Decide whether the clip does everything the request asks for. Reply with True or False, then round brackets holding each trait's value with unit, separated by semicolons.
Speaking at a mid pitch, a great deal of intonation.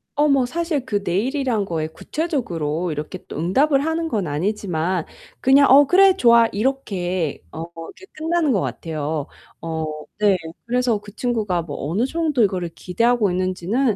False (210 Hz; 7.9 semitones)